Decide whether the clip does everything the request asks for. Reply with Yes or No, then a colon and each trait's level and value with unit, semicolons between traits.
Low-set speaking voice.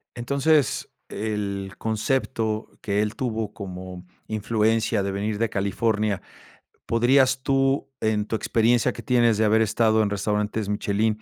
Yes: low, 110 Hz